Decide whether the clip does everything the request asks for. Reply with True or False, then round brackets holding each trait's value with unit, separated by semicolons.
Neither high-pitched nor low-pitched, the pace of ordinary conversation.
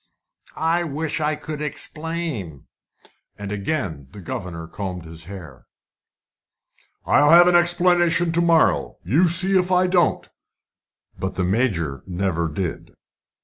False (145 Hz; 125 wpm)